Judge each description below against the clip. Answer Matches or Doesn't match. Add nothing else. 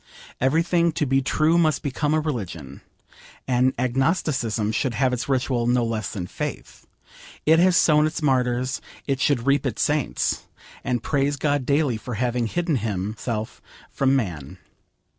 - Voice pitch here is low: Matches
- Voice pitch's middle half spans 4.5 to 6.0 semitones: Doesn't match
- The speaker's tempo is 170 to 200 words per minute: Doesn't match